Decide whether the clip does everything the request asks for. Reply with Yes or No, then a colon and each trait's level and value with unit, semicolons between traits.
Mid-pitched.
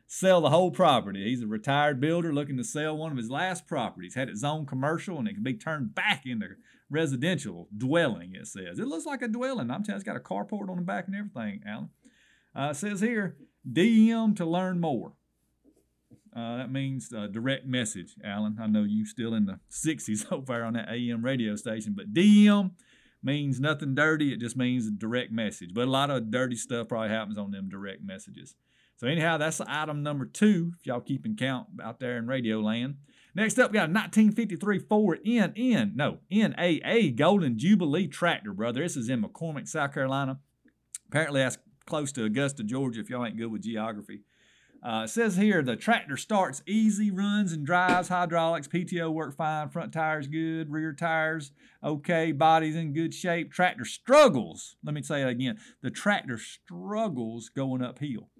Yes: medium, 155 Hz